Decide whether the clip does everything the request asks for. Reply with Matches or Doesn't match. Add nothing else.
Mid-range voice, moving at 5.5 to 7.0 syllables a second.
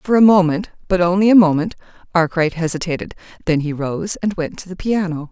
Matches